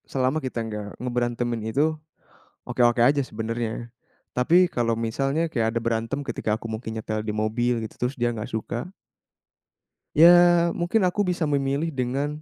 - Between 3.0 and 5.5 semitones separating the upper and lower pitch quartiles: Yes, average, 3.8 semitones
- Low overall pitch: Yes, low, 120 Hz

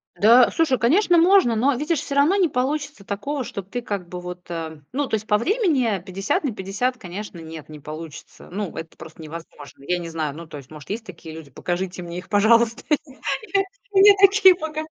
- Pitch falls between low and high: No, high, 210 Hz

